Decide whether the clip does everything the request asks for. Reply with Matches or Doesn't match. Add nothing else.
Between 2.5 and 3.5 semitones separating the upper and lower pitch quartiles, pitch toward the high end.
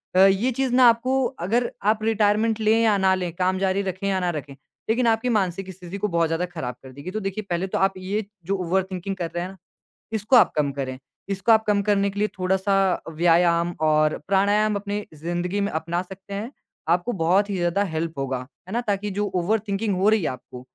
Matches